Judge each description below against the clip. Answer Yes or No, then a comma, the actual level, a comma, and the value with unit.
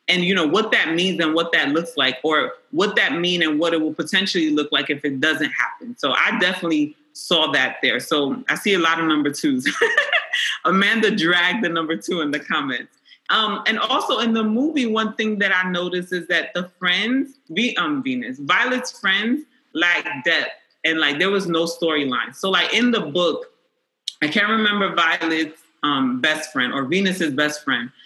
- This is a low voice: No, medium, 180 Hz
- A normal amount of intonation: No, wide, 6.0 semitones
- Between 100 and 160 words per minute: No, average, 200 wpm